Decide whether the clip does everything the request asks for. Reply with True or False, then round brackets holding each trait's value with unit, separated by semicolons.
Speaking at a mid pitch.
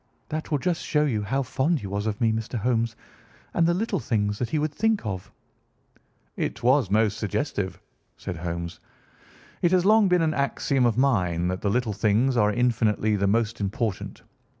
False (115 Hz)